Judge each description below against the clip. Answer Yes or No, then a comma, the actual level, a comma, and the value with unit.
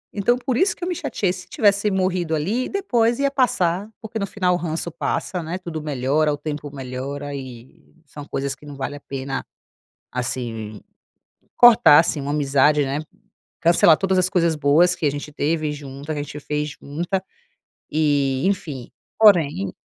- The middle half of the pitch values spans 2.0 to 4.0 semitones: No, average, 4.8 semitones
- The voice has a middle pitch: Yes, medium, 155 Hz